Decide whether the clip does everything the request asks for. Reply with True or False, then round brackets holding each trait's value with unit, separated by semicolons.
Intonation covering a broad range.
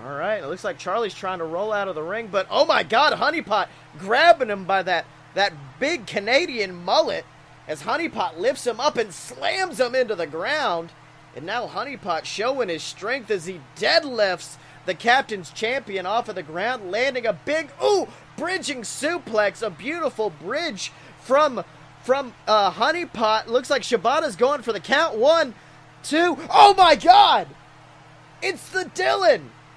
True (8.2 semitones)